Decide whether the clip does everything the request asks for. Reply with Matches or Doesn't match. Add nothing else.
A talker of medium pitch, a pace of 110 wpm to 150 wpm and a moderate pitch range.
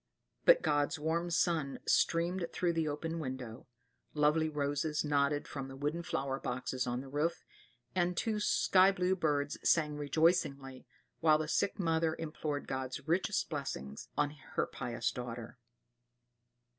Matches